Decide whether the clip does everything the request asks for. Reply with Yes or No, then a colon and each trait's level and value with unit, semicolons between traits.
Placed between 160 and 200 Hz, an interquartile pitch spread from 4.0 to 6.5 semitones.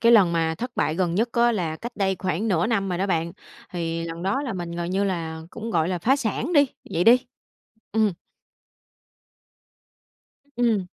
Yes: high, 190 Hz; average, 5.2 semitones